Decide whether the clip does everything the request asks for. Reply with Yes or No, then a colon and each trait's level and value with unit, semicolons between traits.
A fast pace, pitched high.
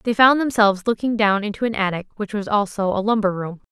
Yes: fast, 225 wpm; high, 210 Hz